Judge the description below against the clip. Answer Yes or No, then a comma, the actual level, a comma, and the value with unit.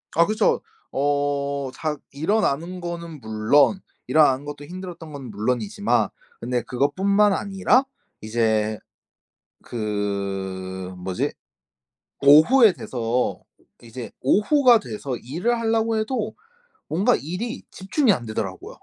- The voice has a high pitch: No, medium, 145 Hz